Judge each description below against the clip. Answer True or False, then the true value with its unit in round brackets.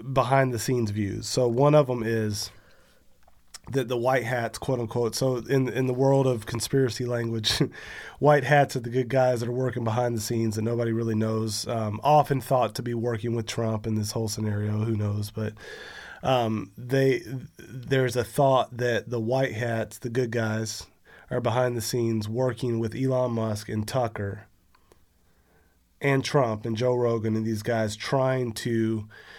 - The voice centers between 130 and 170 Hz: False (120 Hz)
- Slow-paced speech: False (175 wpm)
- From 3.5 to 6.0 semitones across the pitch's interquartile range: False (2.7 semitones)